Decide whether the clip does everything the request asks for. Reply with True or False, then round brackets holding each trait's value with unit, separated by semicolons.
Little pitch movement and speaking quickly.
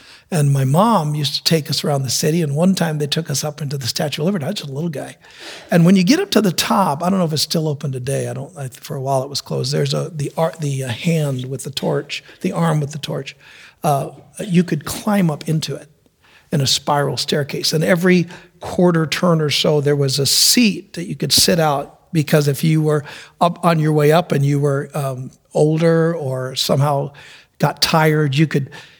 False (3.0 semitones; 235 wpm)